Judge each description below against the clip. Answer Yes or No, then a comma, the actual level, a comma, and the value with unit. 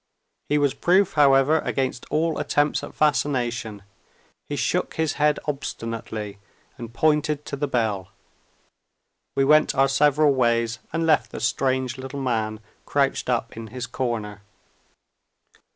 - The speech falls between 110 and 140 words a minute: Yes, slow, 135 wpm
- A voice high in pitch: No, low, 135 Hz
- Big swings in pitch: No, average, 4.1 semitones